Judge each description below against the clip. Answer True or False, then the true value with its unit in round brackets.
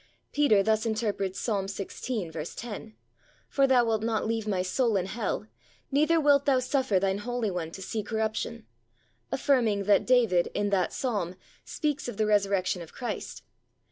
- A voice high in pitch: True (215 Hz)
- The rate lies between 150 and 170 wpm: True (160 wpm)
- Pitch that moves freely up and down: False (4.0 semitones)